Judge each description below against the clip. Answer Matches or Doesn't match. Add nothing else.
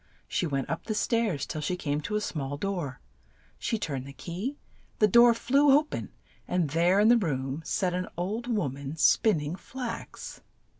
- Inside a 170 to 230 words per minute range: Matches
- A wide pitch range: Matches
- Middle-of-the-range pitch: Matches